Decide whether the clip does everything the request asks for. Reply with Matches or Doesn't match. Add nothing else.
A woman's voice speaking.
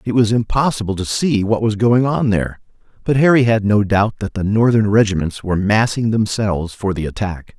Doesn't match